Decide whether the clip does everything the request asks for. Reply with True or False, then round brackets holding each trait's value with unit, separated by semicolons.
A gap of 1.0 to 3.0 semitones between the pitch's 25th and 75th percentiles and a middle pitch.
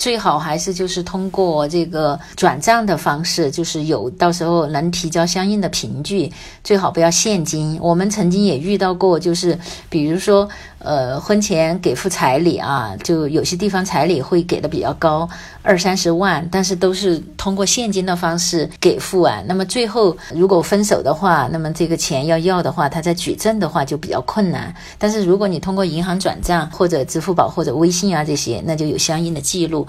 True (2.7 semitones; 175 Hz)